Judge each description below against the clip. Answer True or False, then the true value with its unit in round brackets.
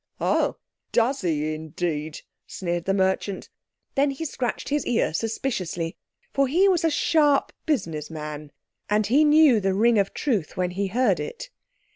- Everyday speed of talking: True (160 wpm)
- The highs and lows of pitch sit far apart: True (8.3 semitones)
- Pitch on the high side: True (205 Hz)